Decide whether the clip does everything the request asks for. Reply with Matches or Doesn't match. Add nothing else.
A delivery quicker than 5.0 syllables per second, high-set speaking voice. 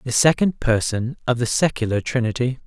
Doesn't match